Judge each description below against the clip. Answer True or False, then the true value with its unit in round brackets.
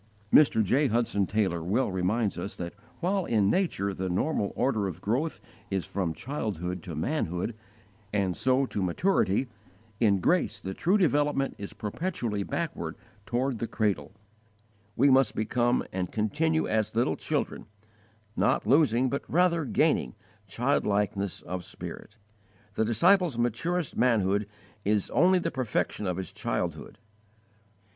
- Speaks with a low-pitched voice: True (110 Hz)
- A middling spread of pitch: False (6.1 semitones)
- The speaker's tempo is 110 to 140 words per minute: True (135 wpm)